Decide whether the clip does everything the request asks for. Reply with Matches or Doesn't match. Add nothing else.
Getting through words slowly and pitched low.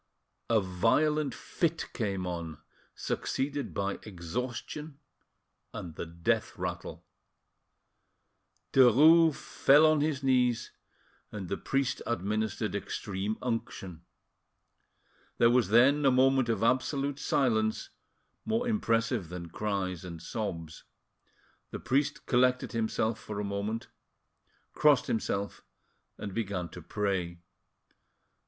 Matches